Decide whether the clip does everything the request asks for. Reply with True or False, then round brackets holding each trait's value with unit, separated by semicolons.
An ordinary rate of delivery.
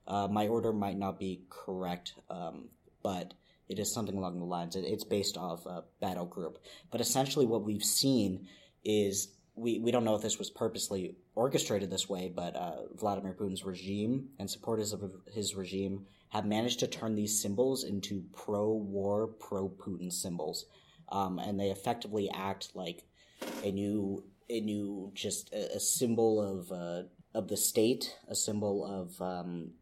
True (165 wpm)